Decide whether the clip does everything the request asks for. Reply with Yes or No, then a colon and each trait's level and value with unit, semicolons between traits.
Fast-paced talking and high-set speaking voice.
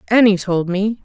No: average, 175 wpm; high, 200 Hz